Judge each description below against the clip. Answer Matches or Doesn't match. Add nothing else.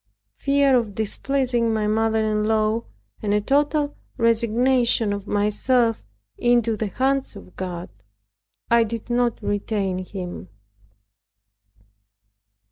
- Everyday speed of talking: Doesn't match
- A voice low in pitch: Doesn't match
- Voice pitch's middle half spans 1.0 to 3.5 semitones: Matches